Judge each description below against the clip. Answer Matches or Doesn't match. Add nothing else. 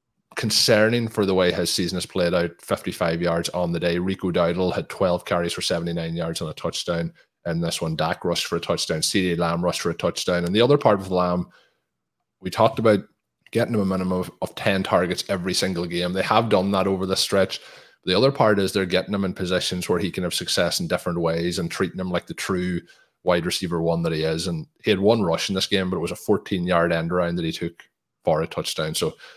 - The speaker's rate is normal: Doesn't match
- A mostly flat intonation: Matches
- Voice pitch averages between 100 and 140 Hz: Doesn't match